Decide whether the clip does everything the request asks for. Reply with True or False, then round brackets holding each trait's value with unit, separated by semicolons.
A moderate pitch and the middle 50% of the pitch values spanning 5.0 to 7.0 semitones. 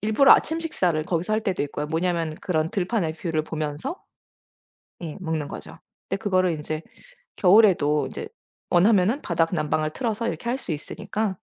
True (175 Hz; 5.4 semitones)